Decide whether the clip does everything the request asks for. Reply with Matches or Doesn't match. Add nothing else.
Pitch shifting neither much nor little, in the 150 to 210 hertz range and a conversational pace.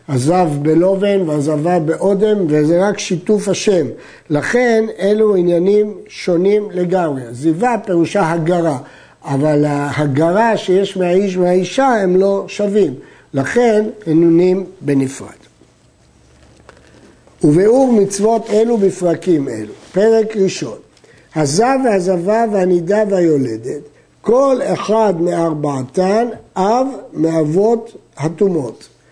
Doesn't match